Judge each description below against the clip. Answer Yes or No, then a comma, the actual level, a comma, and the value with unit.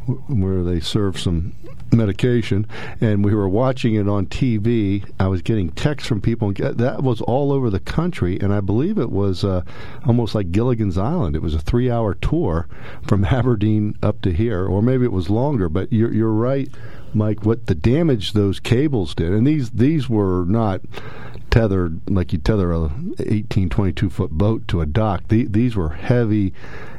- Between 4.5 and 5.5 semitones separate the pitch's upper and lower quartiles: No, average, 3.7 semitones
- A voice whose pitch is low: Yes, low, 110 Hz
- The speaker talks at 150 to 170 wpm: No, average, 180 wpm